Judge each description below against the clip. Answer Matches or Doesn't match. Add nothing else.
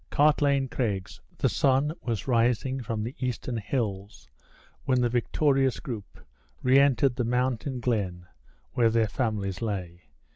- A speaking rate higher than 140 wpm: Doesn't match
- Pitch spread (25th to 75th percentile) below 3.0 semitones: Doesn't match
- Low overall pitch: Matches